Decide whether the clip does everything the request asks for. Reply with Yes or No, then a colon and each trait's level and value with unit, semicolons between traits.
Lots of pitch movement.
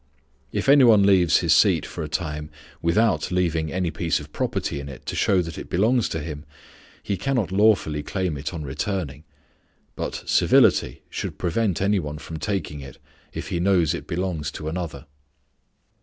No: average, 4.3 semitones